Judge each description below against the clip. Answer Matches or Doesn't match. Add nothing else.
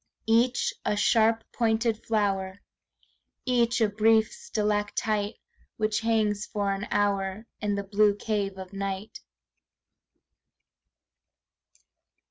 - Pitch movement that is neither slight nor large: Doesn't match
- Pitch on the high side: Matches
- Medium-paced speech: Doesn't match